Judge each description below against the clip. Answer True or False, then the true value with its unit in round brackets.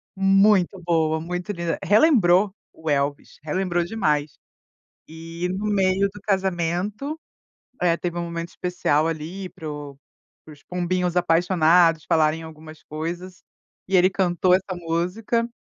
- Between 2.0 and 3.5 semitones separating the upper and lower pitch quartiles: True (2.8 semitones)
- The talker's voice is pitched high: False (175 Hz)